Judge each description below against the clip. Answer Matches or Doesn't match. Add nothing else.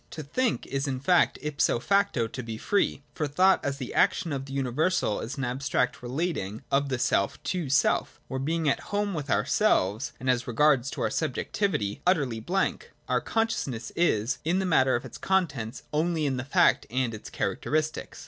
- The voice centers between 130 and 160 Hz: Matches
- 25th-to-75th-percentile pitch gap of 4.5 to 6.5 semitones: Matches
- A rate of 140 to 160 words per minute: Doesn't match